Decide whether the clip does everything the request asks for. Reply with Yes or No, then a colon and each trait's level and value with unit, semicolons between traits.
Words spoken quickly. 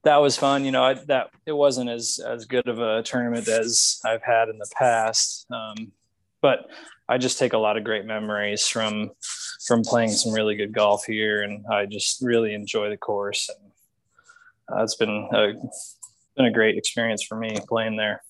No: average, 195 wpm